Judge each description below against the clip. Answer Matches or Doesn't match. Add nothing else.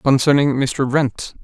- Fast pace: Doesn't match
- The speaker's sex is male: Matches